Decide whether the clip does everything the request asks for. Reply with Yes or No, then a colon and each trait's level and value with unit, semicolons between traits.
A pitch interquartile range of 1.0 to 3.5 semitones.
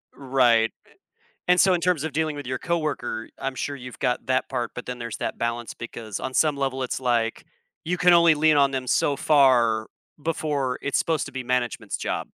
No: average, 3.9 semitones